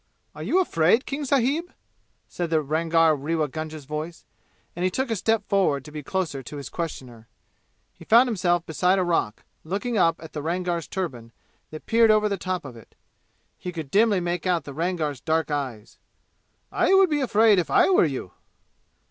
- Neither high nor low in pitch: Yes, medium, 170 Hz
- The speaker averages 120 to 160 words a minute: No, average, 185 wpm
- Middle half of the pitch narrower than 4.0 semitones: No, average, 5.1 semitones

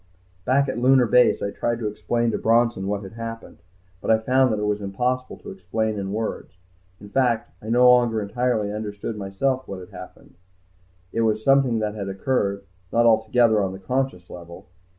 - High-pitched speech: No, low, 110 Hz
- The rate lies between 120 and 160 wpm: No, average, 190 wpm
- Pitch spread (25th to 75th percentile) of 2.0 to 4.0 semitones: Yes, average, 3.3 semitones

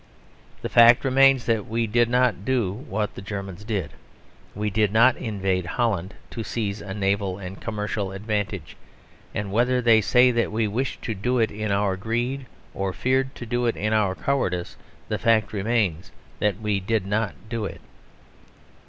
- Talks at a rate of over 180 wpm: No, average, 170 wpm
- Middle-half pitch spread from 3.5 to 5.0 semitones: No, average, 3.1 semitones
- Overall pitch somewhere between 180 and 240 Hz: No, low, 110 Hz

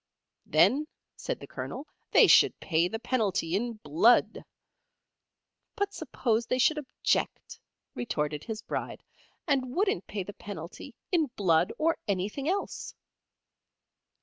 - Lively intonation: Yes, wide, 7.2 semitones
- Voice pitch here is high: Yes, high, 225 Hz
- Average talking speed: No, slow, 120 wpm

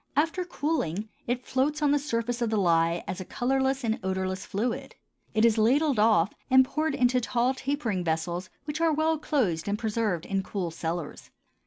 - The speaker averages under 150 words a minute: No, average, 180 wpm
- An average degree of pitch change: No, wide, 6.5 semitones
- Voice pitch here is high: Yes, high, 230 Hz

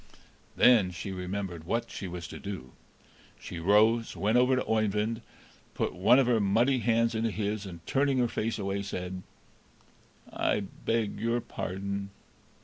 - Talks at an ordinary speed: Yes, average, 150 wpm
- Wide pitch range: No, average, 3.2 semitones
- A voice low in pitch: Yes, low, 105 Hz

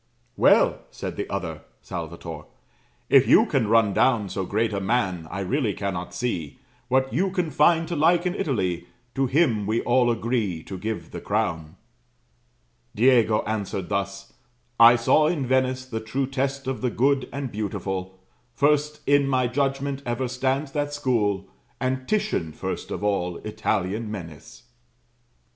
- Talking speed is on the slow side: No, average, 155 wpm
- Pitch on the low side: Yes, low, 120 Hz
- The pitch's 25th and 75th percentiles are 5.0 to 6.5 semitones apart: Yes, wide, 5.4 semitones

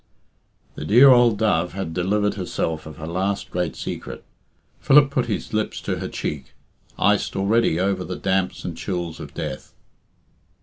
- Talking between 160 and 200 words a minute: Yes, average, 165 wpm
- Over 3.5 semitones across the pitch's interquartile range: Yes, average, 4.1 semitones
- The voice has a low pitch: Yes, very low, 95 Hz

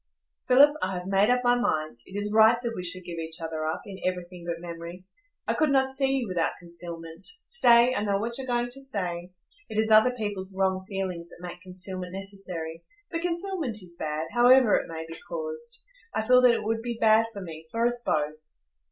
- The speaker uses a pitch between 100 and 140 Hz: No, high, 195 Hz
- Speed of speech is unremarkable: No, fast, 210 wpm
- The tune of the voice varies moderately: No, wide, 5.8 semitones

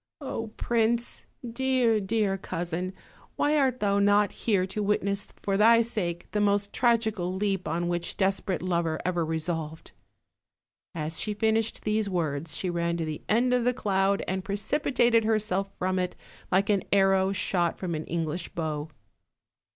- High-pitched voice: Yes, high, 195 Hz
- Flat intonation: No, average, 4.0 semitones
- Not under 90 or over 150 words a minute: No, average, 160 wpm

